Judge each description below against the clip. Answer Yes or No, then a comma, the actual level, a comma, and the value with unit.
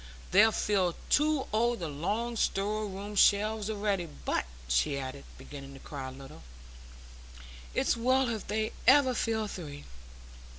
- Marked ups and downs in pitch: Yes, wide, 7.0 semitones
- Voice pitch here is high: Yes, high, 205 Hz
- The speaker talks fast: No, average, 140 wpm